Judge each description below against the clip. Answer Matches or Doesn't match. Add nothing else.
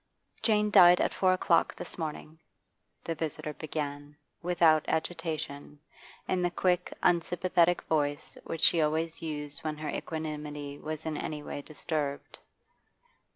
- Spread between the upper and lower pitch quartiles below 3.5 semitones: Matches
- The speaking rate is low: Matches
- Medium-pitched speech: Matches